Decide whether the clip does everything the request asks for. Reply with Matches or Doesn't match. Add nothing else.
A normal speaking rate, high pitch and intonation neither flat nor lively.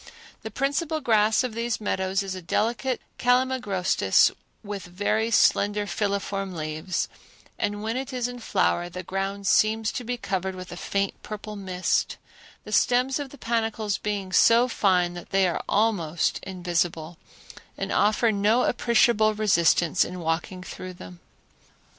Matches